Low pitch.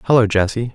Yes: low, 115 Hz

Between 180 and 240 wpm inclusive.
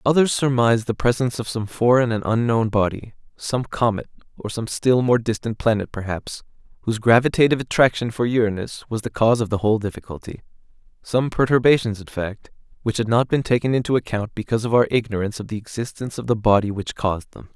Yes: average, 185 wpm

